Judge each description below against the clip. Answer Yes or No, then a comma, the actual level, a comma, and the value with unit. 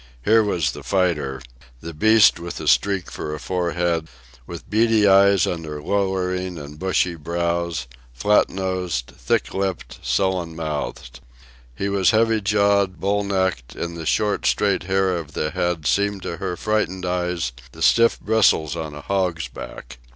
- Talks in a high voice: No, very low, 90 Hz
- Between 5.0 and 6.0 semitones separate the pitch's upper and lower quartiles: No, average, 3.4 semitones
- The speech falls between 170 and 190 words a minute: No, average, 155 wpm